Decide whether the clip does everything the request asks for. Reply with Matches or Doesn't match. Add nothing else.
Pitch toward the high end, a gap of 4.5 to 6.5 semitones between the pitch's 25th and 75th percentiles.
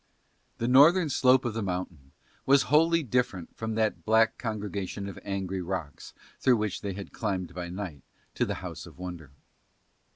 Doesn't match